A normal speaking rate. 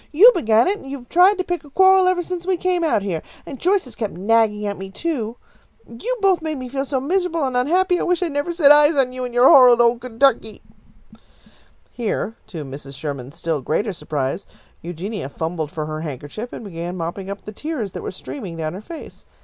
No: fast, 220 wpm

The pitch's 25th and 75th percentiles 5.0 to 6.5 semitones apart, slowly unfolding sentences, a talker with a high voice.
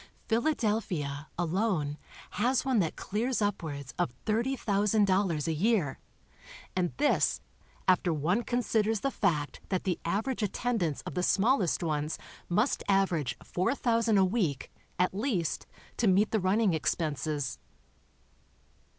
Yes: wide, 5.6 semitones; slow, 125 wpm; high, 195 Hz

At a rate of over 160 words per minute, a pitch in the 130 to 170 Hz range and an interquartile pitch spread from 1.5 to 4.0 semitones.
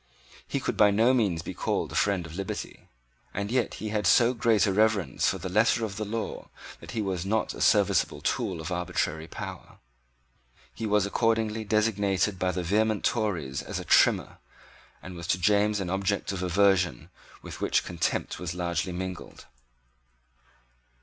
No: average, 170 wpm; low, 100 Hz; average, 3.2 semitones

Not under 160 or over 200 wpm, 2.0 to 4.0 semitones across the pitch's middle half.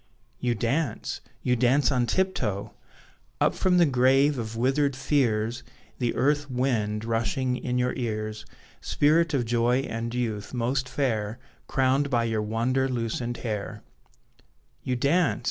No: slow, 135 wpm; average, 3.0 semitones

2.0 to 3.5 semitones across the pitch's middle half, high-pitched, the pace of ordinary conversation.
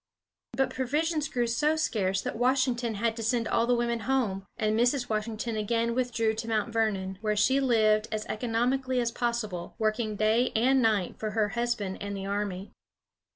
Yes: narrow, 2.4 semitones; high, 230 Hz; average, 175 wpm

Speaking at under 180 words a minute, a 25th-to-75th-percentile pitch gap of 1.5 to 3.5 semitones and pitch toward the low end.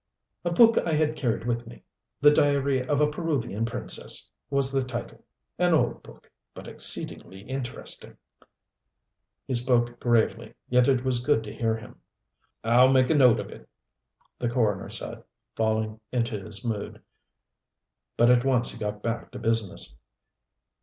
Yes: average, 155 wpm; average, 3.1 semitones; low, 120 Hz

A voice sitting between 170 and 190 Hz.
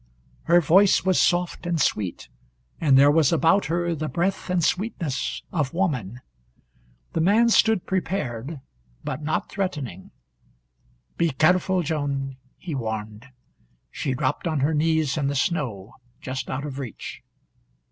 No: medium, 155 Hz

